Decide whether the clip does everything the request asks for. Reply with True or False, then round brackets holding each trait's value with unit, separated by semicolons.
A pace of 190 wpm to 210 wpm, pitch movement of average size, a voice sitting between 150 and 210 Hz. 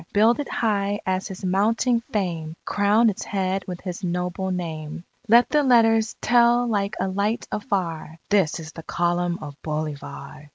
False (160 wpm; 4.2 semitones; 190 Hz)